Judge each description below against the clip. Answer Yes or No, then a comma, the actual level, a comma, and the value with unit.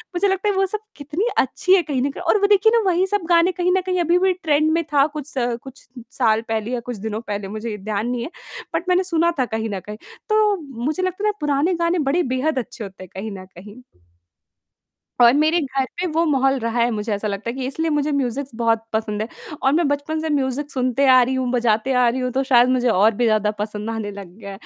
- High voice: Yes, very high, 265 Hz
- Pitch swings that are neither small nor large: No, wide, 6.7 semitones